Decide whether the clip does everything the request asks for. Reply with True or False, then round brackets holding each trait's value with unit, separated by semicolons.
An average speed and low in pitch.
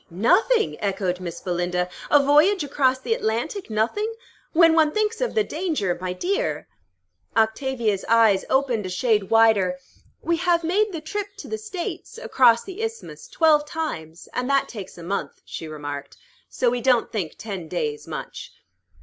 False (160 wpm; 255 Hz)